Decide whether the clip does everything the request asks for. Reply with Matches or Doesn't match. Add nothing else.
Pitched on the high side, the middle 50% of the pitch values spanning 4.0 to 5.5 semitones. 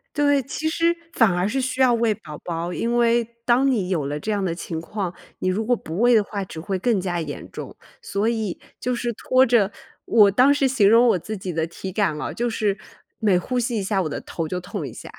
Matches